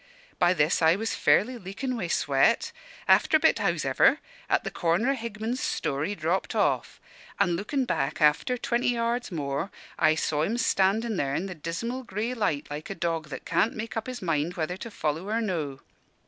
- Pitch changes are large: Yes, wide, 6.7 semitones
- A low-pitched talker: No, high, 190 Hz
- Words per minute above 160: Yes, average, 190 wpm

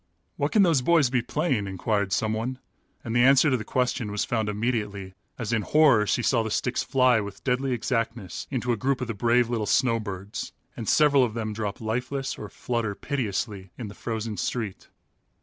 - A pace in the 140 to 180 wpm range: No, average, 190 wpm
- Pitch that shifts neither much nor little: Yes, average, 3.2 semitones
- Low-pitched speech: Yes, low, 115 Hz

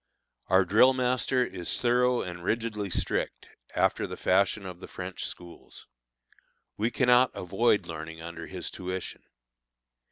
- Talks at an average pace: No, slow, 130 wpm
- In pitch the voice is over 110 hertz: No, very low, 95 Hz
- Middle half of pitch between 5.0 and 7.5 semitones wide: Yes, average, 5.3 semitones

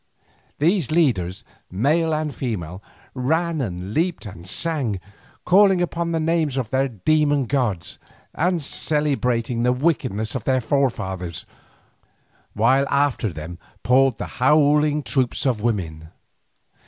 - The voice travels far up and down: Yes, wide, 6.1 semitones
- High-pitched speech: No, low, 135 Hz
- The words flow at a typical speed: No, slow, 120 wpm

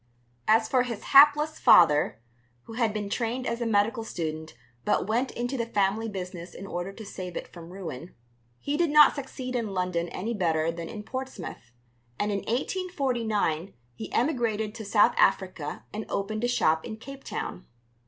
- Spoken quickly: No, average, 175 wpm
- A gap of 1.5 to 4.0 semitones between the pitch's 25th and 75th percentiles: No, average, 5.2 semitones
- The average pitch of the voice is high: Yes, high, 215 Hz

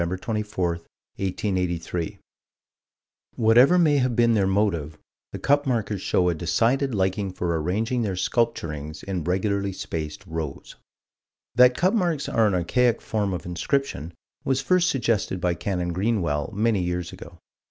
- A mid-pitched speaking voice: No, low, 100 Hz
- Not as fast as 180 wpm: Yes, average, 140 wpm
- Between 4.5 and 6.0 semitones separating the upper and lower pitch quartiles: Yes, average, 5.1 semitones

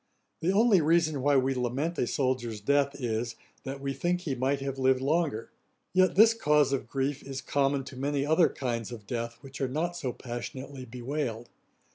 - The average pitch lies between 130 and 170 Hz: Yes, low, 135 Hz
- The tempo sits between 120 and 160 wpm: No, average, 185 wpm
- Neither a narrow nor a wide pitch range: Yes, average, 3.0 semitones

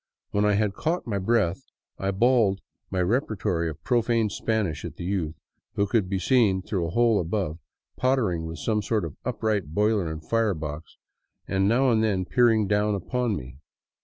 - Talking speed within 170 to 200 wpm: Yes, average, 175 wpm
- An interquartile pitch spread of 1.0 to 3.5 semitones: No, average, 4.1 semitones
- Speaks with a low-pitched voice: Yes, low, 100 Hz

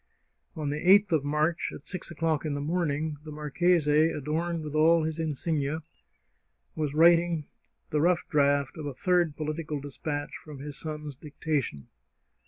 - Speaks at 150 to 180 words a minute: Yes, average, 155 wpm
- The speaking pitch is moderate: Yes, medium, 155 Hz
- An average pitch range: No, narrow, 2.1 semitones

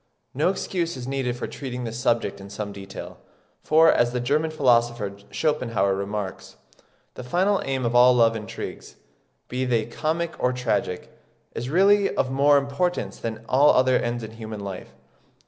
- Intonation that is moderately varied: Yes, average, 4.2 semitones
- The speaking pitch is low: Yes, low, 125 Hz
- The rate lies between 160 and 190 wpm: Yes, average, 165 wpm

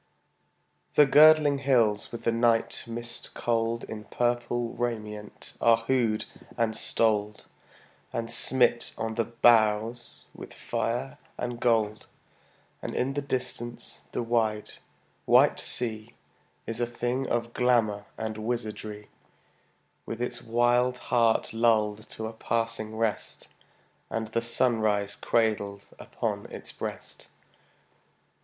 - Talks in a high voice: No, low, 115 Hz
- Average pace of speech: No, slow, 115 wpm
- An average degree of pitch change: No, narrow, 1.7 semitones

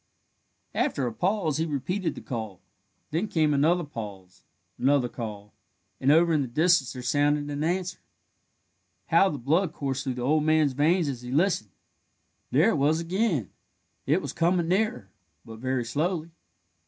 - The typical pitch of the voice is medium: Yes, medium, 150 Hz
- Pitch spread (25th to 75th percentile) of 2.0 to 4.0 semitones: No, average, 5.1 semitones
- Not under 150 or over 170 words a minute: Yes, average, 160 wpm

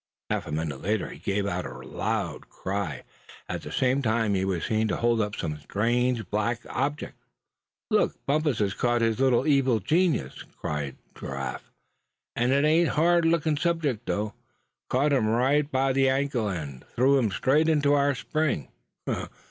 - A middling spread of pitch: No, wide, 5.9 semitones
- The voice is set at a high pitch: No, low, 120 Hz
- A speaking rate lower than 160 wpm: No, average, 165 wpm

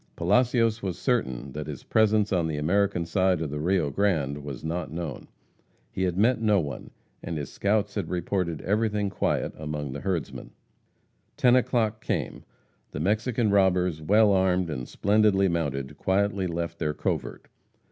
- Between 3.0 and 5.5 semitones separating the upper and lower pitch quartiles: Yes, average, 5.0 semitones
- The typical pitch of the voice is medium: No, very low, 90 Hz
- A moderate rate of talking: Yes, average, 155 wpm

